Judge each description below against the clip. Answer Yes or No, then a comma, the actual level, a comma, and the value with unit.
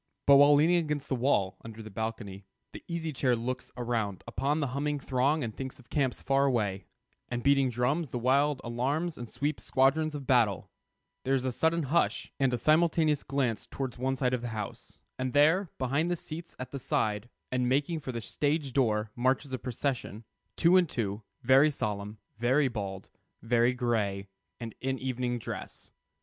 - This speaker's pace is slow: No, average, 185 wpm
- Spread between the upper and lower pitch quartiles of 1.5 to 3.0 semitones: No, average, 3.6 semitones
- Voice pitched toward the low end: Yes, low, 130 Hz